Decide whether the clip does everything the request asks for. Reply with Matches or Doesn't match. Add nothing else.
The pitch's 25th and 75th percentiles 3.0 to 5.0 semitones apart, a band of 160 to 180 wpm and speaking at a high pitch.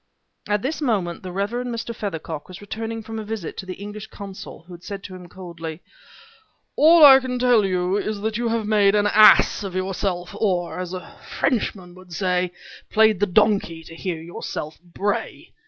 Doesn't match